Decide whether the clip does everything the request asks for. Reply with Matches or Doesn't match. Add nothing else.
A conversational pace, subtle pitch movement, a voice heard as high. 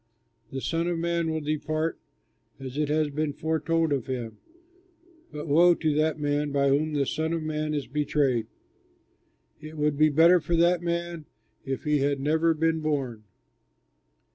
Doesn't match